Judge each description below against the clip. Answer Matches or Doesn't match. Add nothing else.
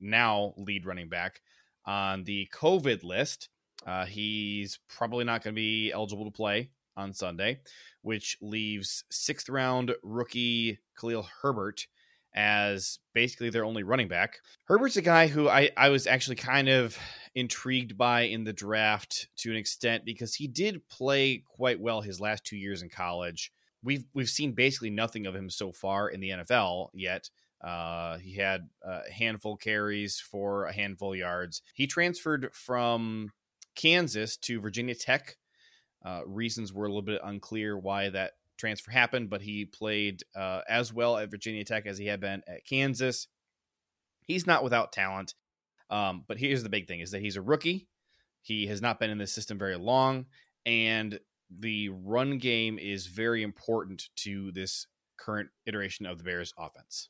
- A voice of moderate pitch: Doesn't match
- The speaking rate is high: Doesn't match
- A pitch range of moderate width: Matches